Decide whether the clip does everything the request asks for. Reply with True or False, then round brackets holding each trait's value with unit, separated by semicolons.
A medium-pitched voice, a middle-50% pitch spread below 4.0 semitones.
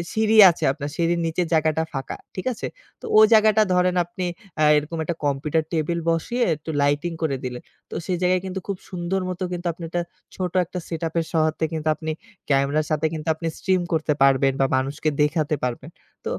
True (160 Hz; 3.0 semitones)